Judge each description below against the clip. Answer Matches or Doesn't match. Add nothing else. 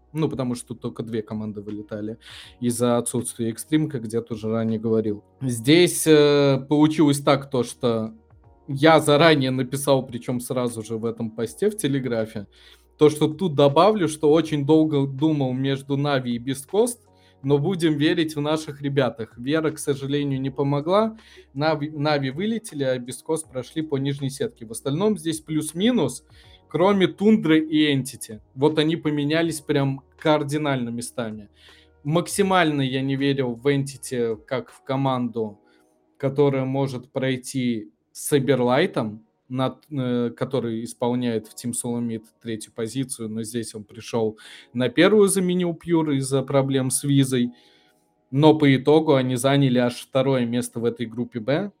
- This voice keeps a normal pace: Matches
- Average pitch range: Matches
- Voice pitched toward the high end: Doesn't match